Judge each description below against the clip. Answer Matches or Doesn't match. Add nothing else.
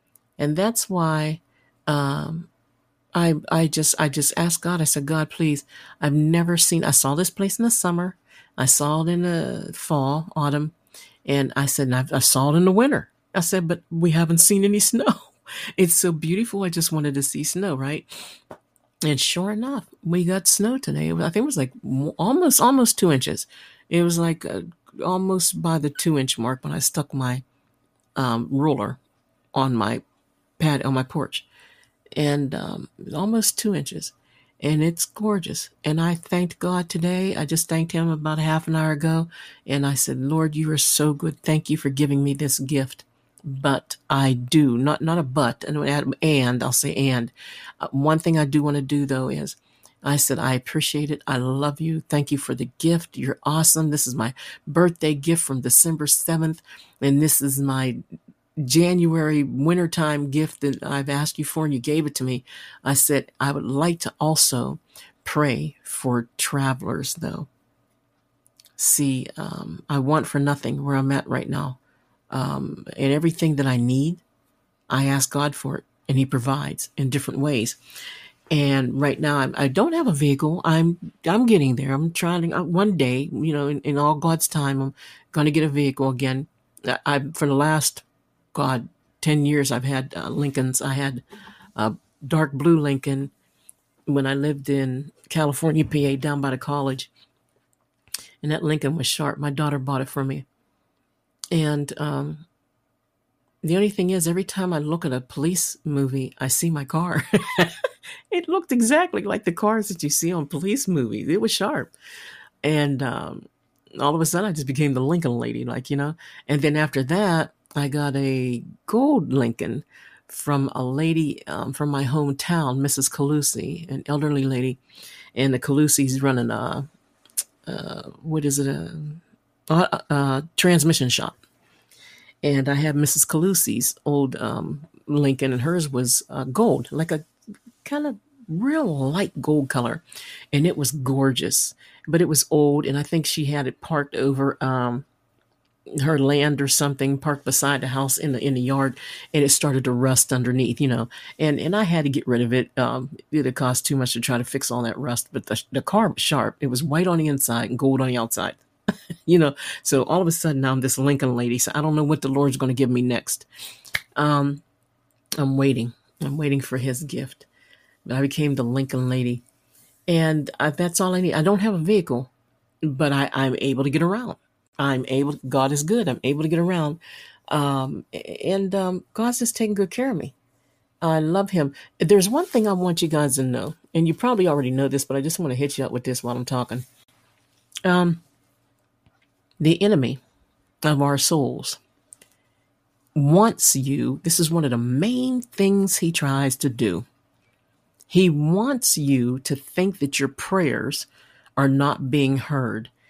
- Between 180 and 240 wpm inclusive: Matches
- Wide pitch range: Doesn't match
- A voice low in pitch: Doesn't match